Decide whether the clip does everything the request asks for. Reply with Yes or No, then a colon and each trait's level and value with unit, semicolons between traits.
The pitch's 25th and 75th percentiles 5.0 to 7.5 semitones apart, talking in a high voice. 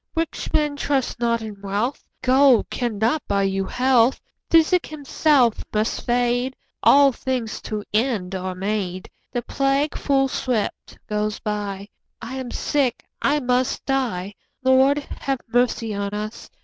No: average, 4.3 semitones; high, 245 Hz